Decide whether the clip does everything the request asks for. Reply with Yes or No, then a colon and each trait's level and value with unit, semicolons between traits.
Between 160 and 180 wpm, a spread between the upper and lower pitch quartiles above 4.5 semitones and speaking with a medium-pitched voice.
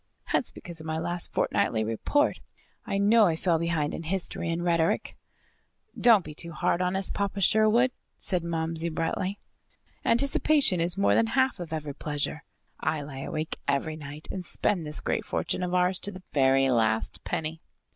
No: average, 175 wpm; average, 3.8 semitones; medium, 170 Hz